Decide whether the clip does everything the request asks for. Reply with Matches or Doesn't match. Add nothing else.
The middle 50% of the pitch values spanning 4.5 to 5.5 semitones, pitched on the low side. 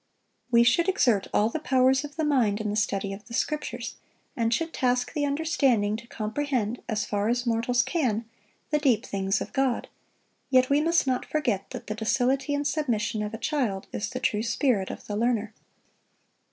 Doesn't match